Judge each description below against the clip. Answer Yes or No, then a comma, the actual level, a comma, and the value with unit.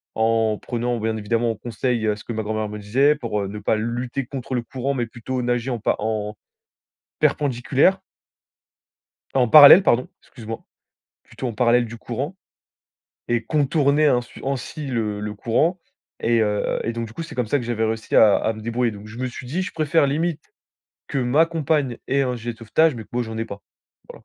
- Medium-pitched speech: No, low, 120 Hz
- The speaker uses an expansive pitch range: No, average, 3.6 semitones